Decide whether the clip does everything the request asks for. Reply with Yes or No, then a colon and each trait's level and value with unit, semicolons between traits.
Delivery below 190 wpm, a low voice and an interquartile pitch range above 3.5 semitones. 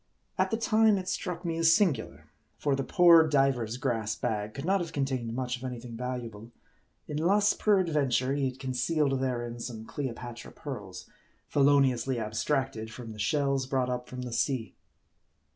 Yes: average, 165 wpm; low, 130 Hz; average, 4.1 semitones